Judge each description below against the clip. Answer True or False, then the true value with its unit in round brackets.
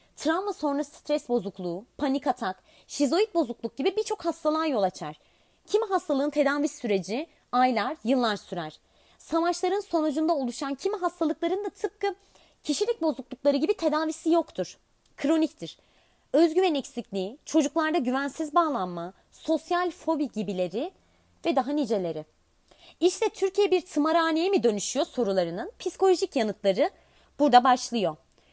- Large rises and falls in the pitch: True (5.9 semitones)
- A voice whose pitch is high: True (295 Hz)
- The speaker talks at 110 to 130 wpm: True (115 wpm)